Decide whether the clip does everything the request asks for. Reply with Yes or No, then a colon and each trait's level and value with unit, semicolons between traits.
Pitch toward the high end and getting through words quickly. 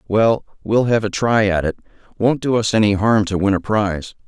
No: low, 105 Hz; fast, 225 wpm